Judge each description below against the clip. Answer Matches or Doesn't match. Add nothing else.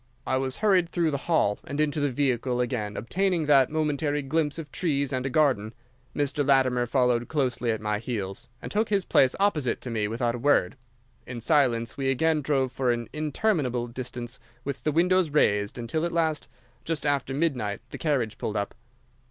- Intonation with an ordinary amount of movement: Matches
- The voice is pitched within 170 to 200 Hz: Doesn't match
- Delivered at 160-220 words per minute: Matches